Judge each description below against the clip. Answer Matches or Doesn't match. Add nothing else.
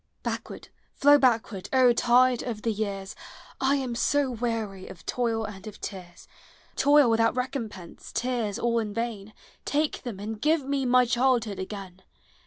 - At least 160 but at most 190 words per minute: Matches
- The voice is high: Matches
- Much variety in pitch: Doesn't match